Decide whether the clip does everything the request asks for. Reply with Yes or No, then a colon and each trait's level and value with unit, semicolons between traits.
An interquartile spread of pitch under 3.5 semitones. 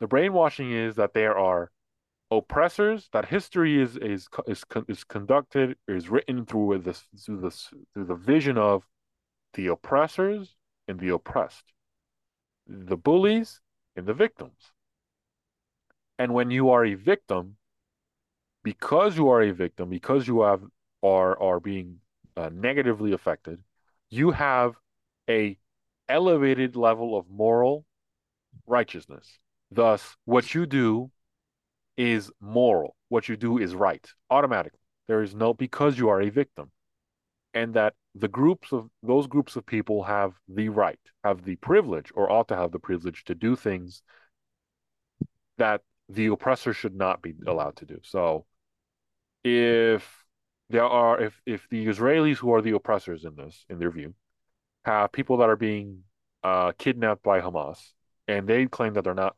No: average, 4.5 semitones